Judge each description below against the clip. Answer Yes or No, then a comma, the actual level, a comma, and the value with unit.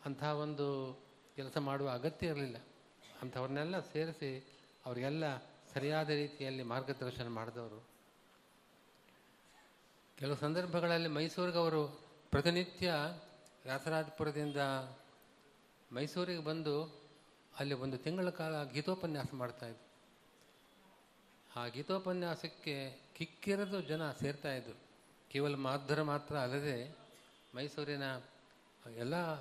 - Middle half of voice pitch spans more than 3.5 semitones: No, average, 2.8 semitones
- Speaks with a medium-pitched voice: Yes, medium, 145 Hz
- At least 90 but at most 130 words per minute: No, average, 75 wpm